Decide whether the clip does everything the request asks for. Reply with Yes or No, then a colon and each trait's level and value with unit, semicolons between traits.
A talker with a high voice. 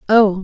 Yes: high, 205 Hz